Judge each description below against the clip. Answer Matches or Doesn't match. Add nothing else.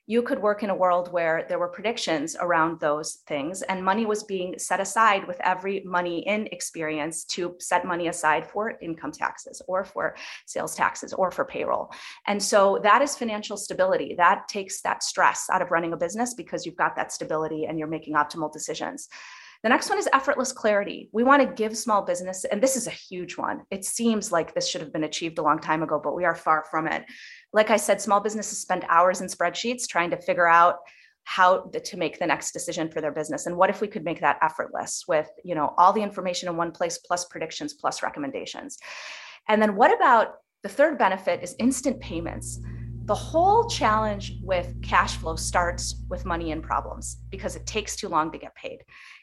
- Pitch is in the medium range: Matches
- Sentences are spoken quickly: Matches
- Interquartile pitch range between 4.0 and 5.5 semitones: Matches